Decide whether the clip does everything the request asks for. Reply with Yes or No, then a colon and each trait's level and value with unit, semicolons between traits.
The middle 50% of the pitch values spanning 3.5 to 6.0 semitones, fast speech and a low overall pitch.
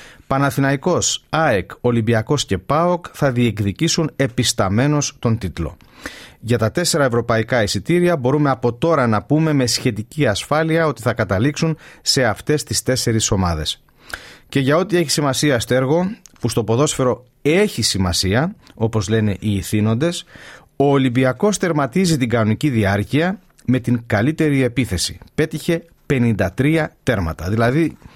No: average, 5.2 semitones; average, 130 wpm; low, 130 Hz